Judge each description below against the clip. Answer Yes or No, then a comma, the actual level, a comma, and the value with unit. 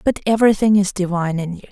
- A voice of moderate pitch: No, high, 195 Hz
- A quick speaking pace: Yes, fast, 210 wpm